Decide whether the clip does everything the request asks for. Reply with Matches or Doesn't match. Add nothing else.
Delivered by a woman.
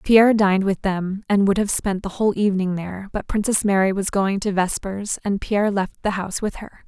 Matches